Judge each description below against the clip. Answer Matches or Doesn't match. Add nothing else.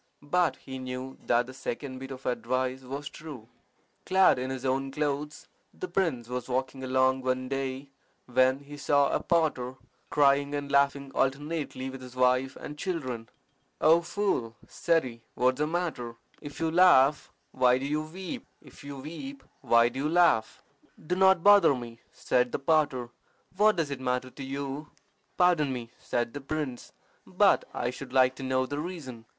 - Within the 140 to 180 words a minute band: Matches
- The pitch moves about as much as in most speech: Matches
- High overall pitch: Doesn't match